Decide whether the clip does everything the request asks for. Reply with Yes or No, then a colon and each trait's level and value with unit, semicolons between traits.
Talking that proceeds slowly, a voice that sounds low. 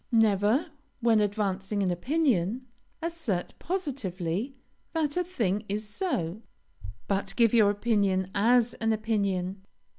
No: slow, 115 wpm; high, 215 Hz